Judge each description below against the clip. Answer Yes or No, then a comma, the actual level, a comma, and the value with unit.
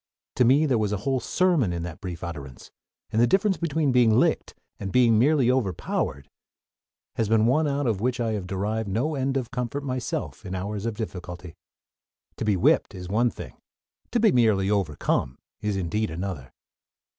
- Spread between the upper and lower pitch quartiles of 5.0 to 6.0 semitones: Yes, wide, 5.4 semitones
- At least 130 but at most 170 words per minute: No, average, 180 wpm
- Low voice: Yes, low, 110 Hz